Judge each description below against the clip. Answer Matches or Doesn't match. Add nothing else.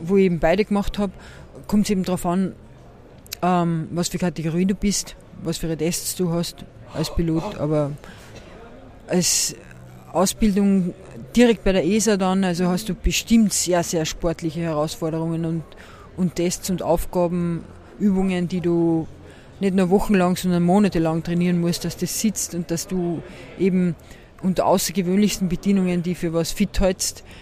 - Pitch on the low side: Doesn't match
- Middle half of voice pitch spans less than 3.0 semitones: Matches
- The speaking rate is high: Doesn't match